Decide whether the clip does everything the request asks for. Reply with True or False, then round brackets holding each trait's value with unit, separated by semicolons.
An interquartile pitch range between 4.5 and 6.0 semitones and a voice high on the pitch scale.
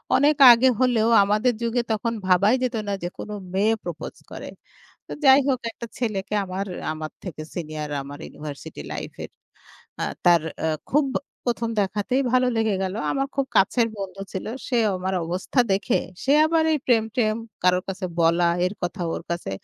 True (5.2 semitones; 205 Hz)